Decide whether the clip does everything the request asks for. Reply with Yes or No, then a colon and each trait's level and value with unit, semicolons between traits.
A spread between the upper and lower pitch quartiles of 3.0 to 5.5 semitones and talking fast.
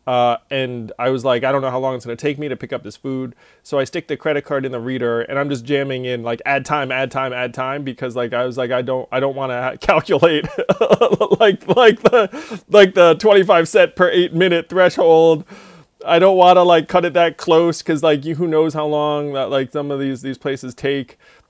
Yes: average, 4.2 semitones; fast, 245 wpm